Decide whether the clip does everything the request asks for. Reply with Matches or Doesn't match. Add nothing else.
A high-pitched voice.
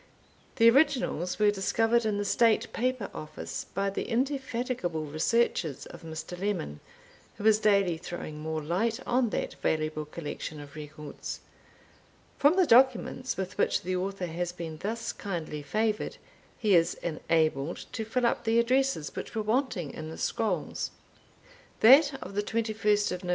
Matches